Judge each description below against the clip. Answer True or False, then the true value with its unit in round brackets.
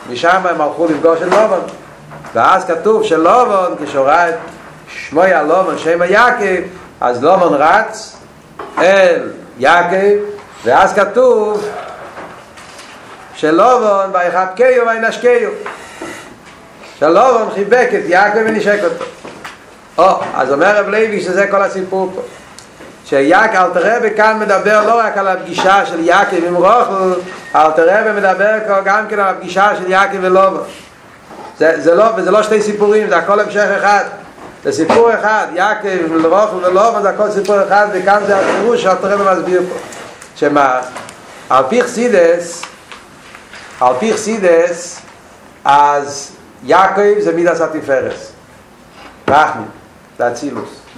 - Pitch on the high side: True (195 Hz)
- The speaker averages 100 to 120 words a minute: False (130 wpm)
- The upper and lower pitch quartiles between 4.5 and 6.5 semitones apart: False (3.4 semitones)